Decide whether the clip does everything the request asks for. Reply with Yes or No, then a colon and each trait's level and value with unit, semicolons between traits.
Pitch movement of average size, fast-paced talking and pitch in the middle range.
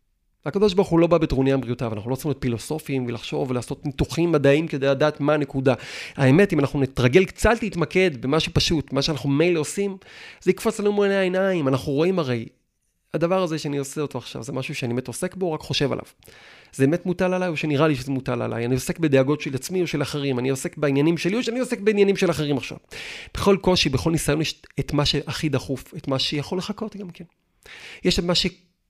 Yes: average, 5.0 semitones; fast, 190 wpm; medium, 150 Hz